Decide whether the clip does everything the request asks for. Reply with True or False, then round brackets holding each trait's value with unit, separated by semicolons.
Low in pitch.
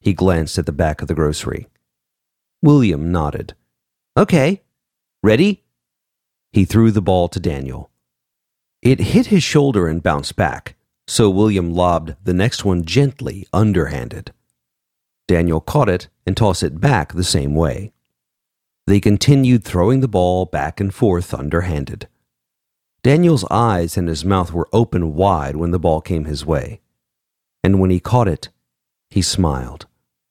True (90 Hz)